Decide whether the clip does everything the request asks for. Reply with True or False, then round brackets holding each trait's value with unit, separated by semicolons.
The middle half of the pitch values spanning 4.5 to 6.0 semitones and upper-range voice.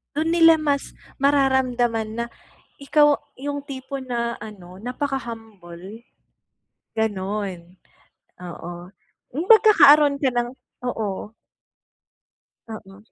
True (5.3 semitones; 240 Hz)